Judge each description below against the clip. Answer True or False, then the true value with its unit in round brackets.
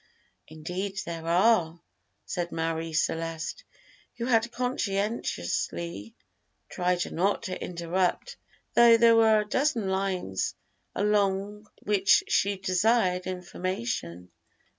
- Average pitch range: True (4.1 semitones)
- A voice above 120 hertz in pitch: True (185 Hz)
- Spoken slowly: True (95 wpm)